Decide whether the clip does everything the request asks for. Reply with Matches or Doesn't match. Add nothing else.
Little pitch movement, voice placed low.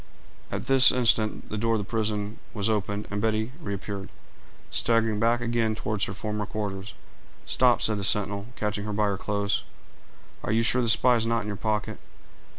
Matches